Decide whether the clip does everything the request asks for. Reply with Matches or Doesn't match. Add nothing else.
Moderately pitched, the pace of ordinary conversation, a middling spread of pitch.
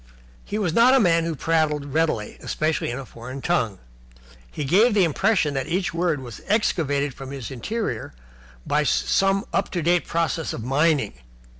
Matches